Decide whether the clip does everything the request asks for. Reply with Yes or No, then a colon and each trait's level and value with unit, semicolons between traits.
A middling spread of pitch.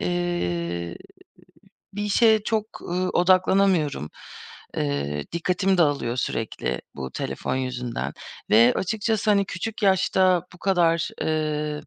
No: wide, 7.4 semitones